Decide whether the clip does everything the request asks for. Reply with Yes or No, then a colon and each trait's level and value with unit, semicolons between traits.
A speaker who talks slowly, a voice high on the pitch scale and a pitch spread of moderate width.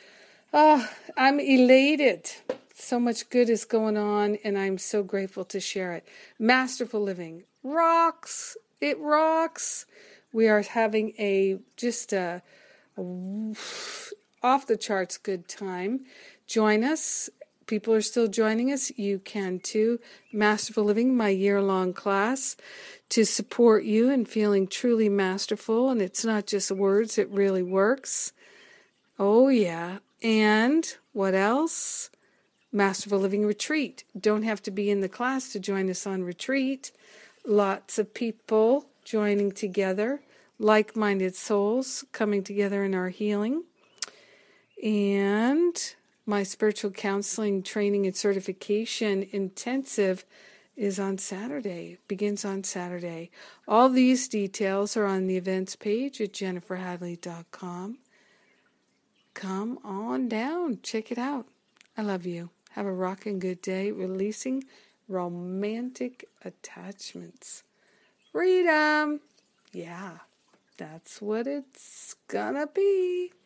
Yes: slow, 120 wpm; high, 210 Hz; average, 3.8 semitones